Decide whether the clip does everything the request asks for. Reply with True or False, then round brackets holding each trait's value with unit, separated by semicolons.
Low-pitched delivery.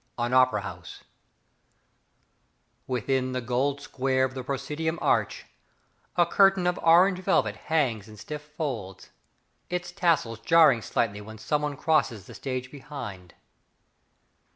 True (130 Hz)